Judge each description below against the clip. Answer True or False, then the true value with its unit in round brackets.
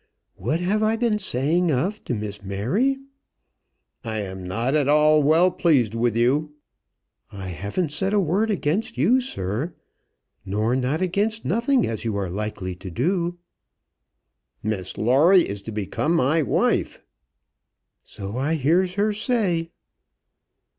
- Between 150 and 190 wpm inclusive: False (140 wpm)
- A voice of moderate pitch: True (150 Hz)